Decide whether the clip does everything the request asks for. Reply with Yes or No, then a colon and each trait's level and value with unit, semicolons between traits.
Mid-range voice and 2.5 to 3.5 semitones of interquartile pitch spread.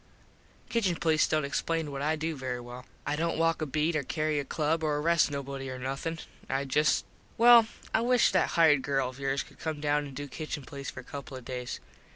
Yes: medium, 150 Hz; average, 3.0 semitones